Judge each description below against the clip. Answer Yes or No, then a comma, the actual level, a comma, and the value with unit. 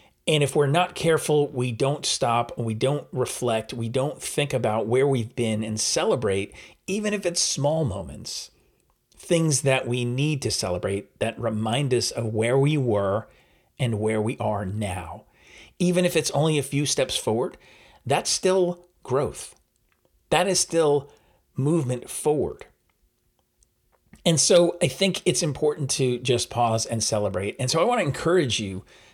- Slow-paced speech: No, average, 160 wpm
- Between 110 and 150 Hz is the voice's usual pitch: Yes, low, 135 Hz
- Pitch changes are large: Yes, wide, 6.4 semitones